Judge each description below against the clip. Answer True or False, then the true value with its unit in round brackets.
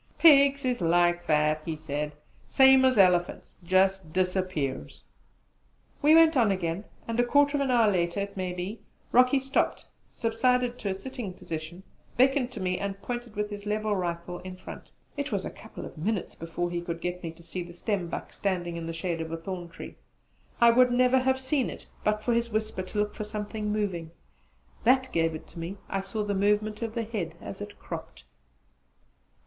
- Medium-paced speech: True (195 wpm)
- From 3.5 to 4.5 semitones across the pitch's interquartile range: False (5.5 semitones)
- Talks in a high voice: True (200 Hz)